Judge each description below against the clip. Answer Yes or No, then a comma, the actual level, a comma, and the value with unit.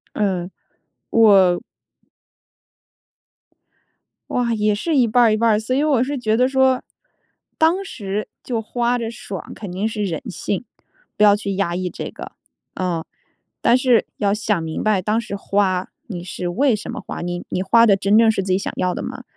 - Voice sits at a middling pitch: No, high, 210 Hz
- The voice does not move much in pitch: No, average, 3.8 semitones